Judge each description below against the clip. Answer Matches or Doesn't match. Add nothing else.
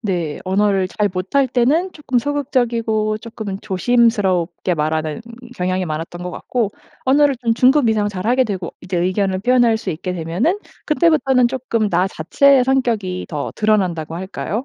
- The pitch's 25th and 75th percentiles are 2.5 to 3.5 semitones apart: Doesn't match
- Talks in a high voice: Matches